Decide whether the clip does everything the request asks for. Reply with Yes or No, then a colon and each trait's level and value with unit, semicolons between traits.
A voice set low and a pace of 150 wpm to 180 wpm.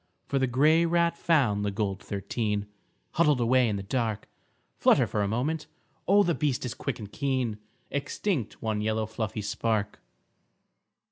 Yes: low, 115 Hz; average, 155 wpm